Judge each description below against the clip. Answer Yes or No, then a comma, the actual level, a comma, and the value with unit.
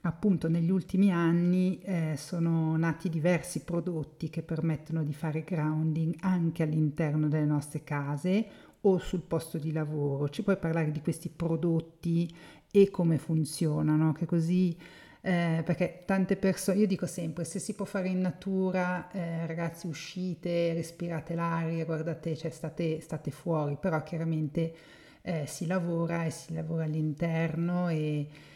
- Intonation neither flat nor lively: No, narrow, 2.1 semitones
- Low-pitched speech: No, medium, 165 Hz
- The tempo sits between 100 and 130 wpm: No, average, 145 wpm